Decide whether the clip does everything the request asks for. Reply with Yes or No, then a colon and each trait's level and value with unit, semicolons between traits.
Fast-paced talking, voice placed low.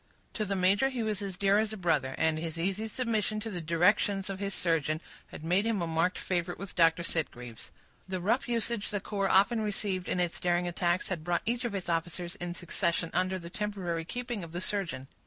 No: fast, 215 wpm; medium, 185 Hz